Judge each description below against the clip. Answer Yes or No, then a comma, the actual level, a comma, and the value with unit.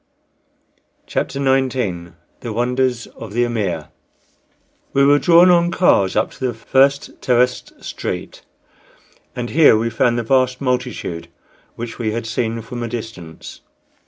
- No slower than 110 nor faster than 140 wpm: Yes, slow, 135 wpm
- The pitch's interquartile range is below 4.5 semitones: Yes, average, 2.8 semitones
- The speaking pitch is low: Yes, low, 120 Hz